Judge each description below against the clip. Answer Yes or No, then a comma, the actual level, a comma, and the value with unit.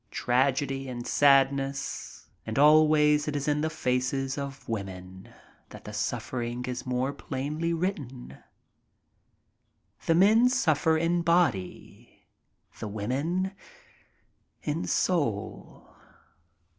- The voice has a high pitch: No, medium, 140 Hz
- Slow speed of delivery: Yes, slow, 105 wpm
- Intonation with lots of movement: No, average, 4.1 semitones